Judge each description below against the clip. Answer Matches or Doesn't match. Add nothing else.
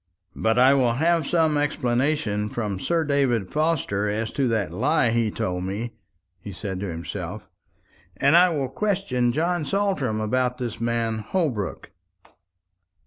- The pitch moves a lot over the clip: Matches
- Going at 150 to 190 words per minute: Doesn't match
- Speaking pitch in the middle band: Doesn't match